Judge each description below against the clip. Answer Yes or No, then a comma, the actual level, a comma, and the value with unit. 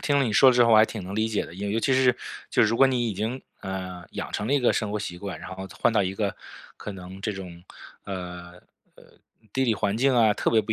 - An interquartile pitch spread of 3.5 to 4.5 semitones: Yes, average, 3.8 semitones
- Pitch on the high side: No, low, 105 Hz